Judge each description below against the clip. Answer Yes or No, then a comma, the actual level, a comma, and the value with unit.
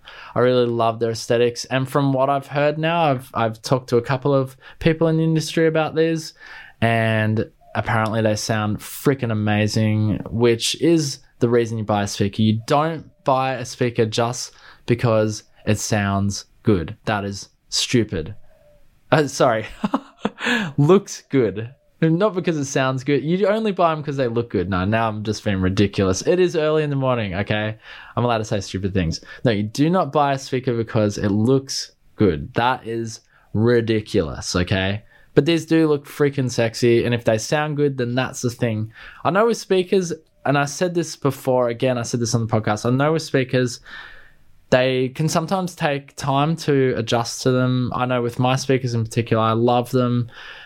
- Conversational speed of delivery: Yes, average, 185 wpm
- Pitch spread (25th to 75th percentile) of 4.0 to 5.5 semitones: Yes, average, 4.7 semitones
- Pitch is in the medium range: No, low, 125 Hz